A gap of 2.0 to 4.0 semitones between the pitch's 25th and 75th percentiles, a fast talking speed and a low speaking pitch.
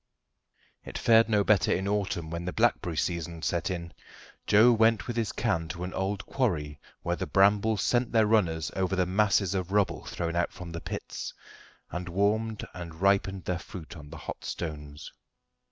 No: average, 3.7 semitones; average, 180 wpm; very low, 95 Hz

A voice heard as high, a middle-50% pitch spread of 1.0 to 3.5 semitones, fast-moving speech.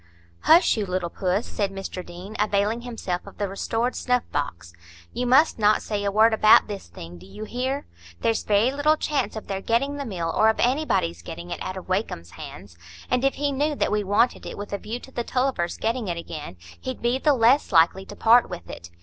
No: high, 215 Hz; average, 5.3 semitones; fast, 220 wpm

